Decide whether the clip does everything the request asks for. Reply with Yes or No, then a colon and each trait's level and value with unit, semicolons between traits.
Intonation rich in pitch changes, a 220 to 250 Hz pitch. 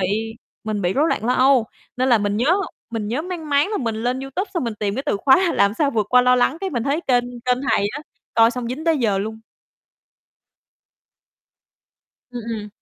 No: average, 4.3 semitones; high, 245 Hz